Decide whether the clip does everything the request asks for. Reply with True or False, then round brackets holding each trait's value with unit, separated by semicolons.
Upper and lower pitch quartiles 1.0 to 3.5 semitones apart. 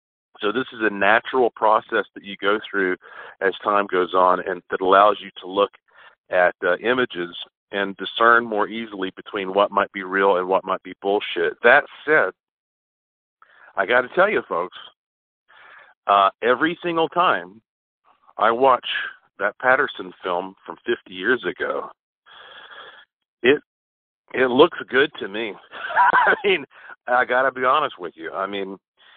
False (5.4 semitones)